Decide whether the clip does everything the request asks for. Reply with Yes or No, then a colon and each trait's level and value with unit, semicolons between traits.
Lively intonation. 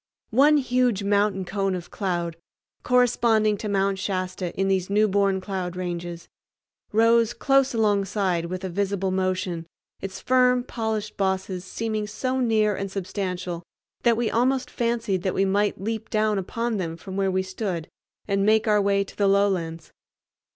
No: average, 2.9 semitones